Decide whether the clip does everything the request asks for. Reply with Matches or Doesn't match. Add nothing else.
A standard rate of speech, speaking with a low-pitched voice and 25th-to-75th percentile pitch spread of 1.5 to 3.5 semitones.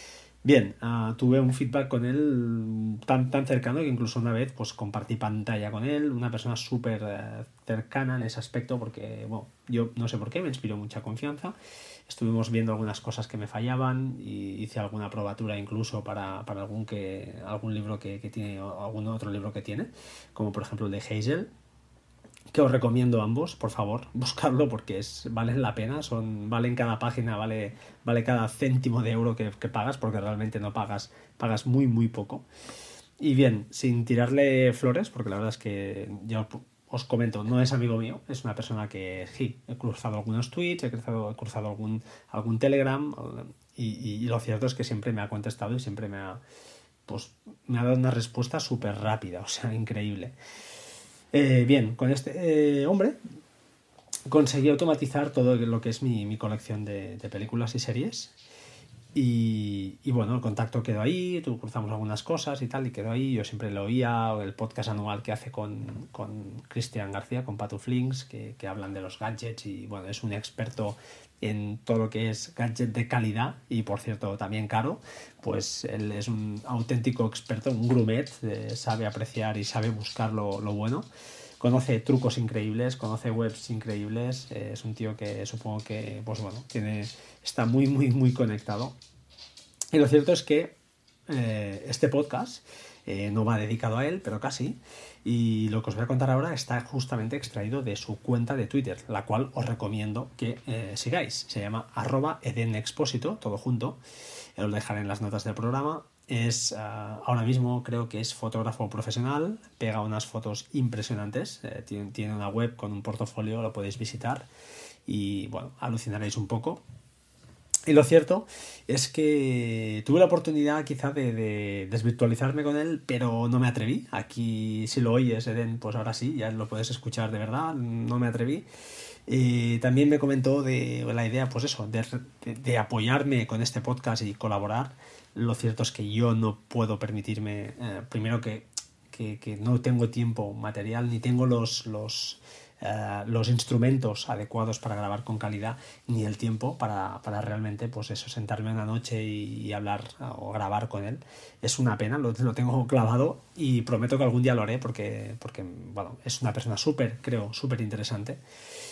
Matches